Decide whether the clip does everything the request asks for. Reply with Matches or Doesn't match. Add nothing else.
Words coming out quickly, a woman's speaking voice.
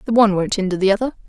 Matches